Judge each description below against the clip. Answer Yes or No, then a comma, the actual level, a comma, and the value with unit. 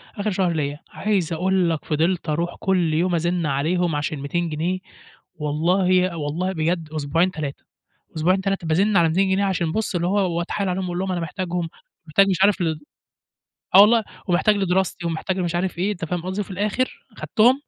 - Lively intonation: No, average, 2.7 semitones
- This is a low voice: No, medium, 180 Hz